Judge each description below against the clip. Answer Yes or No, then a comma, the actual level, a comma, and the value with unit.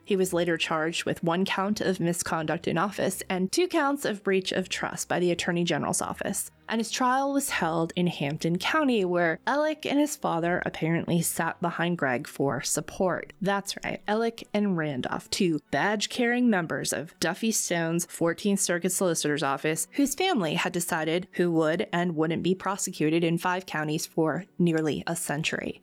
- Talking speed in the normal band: Yes, average, 170 wpm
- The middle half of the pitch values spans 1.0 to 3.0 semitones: No, average, 3.7 semitones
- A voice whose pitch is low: No, medium, 175 Hz